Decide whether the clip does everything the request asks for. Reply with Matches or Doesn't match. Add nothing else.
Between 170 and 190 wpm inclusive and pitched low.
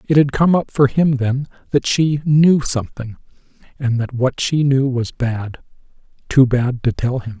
Matches